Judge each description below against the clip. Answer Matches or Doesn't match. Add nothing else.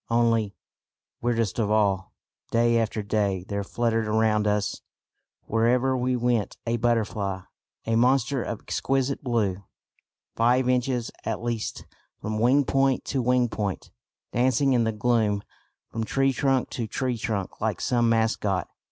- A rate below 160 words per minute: Matches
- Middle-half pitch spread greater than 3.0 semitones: Doesn't match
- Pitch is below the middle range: Matches